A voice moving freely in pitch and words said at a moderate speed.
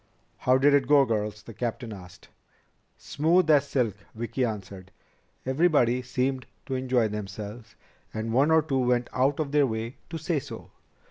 No: average, 4.2 semitones; average, 160 wpm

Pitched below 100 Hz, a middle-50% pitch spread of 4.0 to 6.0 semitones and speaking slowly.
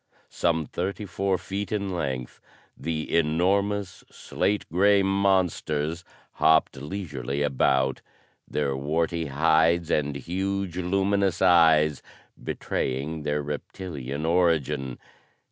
Yes: very low, 80 Hz; average, 4.6 semitones; slow, 95 wpm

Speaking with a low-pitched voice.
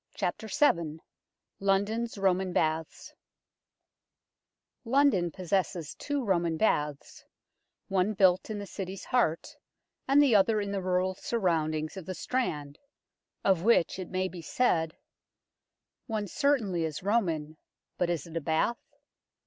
No: medium, 185 Hz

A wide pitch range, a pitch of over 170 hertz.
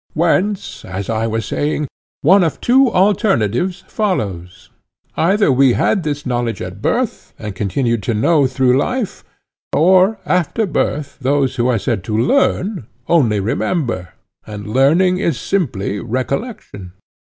No: wide, 8.9 semitones; low, 135 Hz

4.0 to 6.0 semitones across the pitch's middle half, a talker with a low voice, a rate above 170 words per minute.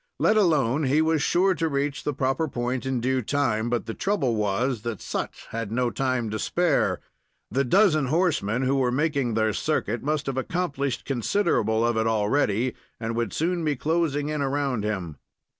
Yes: average, 4.8 semitones; low, 130 Hz; average, 180 wpm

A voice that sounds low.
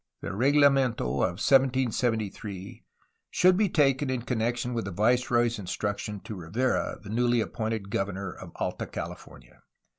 Yes: low, 115 Hz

